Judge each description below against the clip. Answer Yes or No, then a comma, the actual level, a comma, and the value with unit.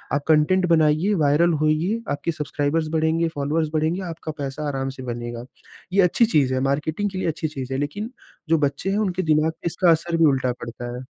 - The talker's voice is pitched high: No, medium, 155 Hz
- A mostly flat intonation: No, average, 3.1 semitones